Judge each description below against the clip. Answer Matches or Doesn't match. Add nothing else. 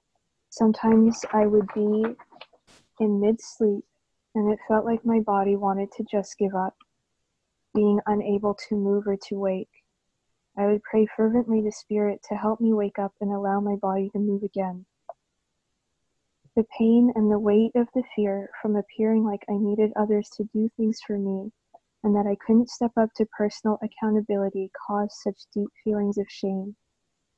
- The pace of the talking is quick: Doesn't match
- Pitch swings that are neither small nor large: Doesn't match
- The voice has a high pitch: Matches